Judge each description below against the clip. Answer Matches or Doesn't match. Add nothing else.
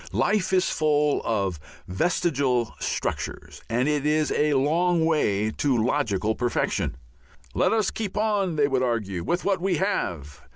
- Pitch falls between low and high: Matches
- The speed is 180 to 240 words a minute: Doesn't match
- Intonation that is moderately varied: Doesn't match